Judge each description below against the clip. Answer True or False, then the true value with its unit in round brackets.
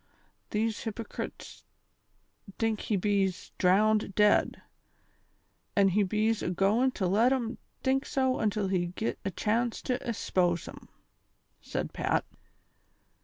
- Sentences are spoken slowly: True (120 wpm)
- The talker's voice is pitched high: True (210 Hz)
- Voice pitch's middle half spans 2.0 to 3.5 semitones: True (2.9 semitones)